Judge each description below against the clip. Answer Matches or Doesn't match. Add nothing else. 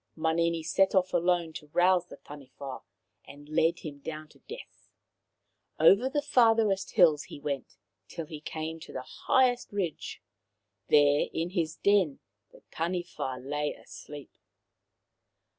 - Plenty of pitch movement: Doesn't match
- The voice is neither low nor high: Matches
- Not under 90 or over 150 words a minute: Matches